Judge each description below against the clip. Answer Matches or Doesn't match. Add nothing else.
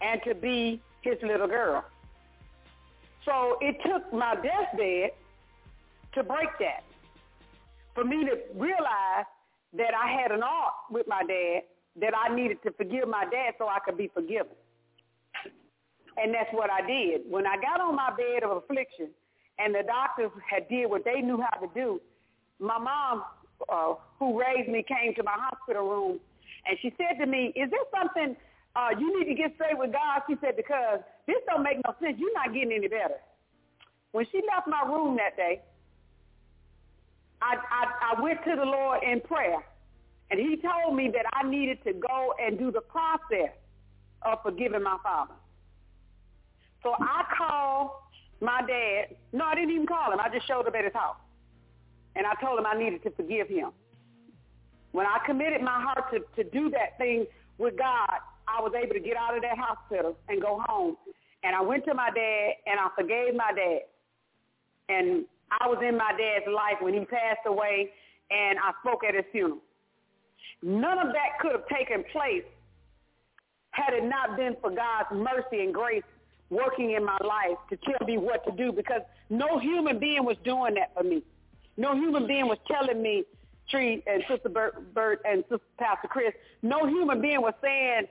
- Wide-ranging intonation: Matches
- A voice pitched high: Matches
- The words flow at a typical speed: Matches